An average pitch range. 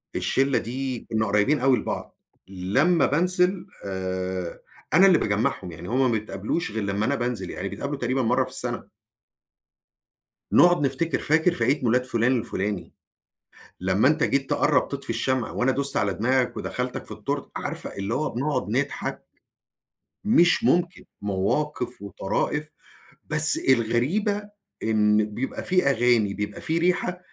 No: wide, 6.0 semitones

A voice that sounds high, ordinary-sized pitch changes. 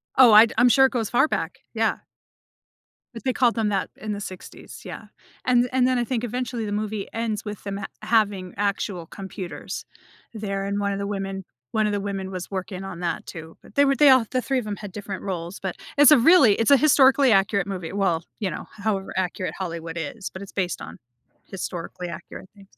Yes: high, 205 Hz; average, 3.6 semitones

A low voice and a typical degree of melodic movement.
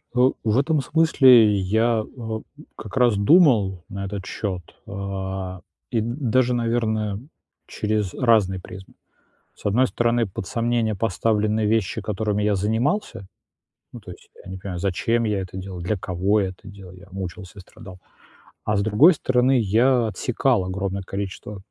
Yes: low, 105 Hz; average, 3.5 semitones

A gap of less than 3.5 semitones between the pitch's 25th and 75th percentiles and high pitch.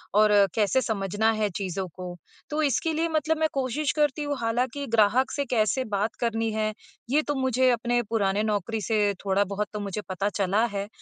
No: average, 4.3 semitones; high, 225 Hz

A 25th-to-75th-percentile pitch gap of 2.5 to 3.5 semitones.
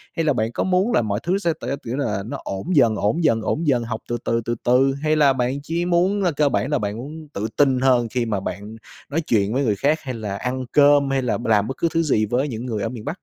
No: average, 5.1 semitones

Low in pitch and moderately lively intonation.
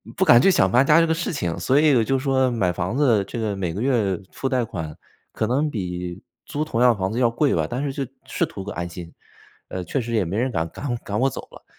No: low, 115 Hz; wide, 6.2 semitones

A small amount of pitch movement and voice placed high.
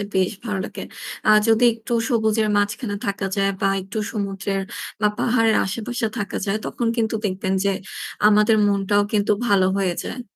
Yes: narrow, 2.2 semitones; high, 205 Hz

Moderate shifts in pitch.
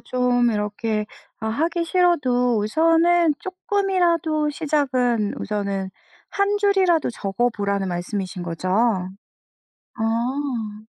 No: wide, 7.9 semitones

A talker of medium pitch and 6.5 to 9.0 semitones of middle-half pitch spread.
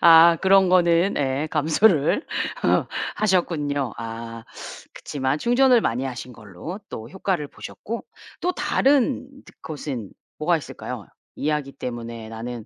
Yes: medium, 150 Hz; wide, 7.5 semitones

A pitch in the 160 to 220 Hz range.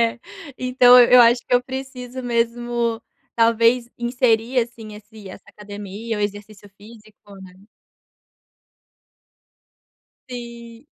No: high, 235 Hz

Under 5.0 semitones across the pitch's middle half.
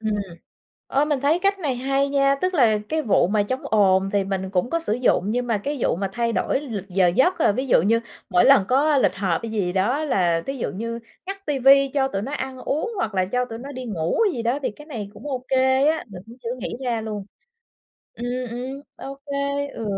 No: average, 5.3 semitones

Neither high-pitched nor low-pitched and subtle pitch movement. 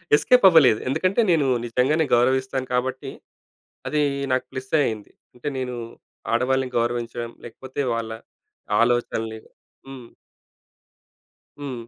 No: low, 130 Hz; narrow, 2.3 semitones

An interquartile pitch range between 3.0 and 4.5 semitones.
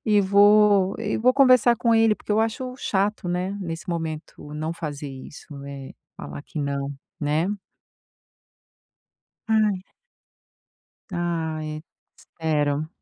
No: wide, 5.6 semitones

